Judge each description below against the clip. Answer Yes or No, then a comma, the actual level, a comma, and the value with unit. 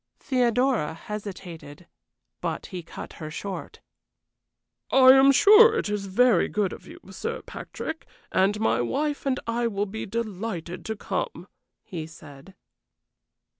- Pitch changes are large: Yes, wide, 6.0 semitones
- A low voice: No, high, 210 Hz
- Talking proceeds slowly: Yes, slow, 130 wpm